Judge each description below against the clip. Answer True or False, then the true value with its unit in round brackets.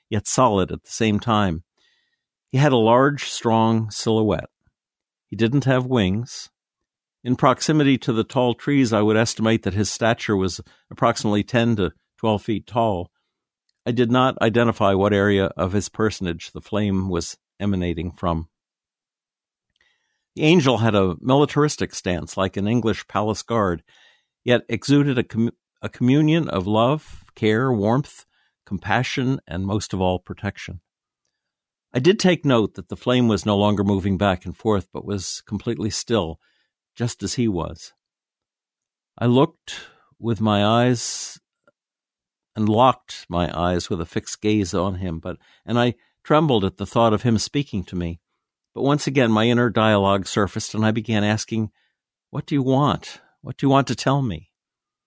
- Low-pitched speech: True (110 Hz)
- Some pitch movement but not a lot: True (4.0 semitones)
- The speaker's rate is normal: True (160 wpm)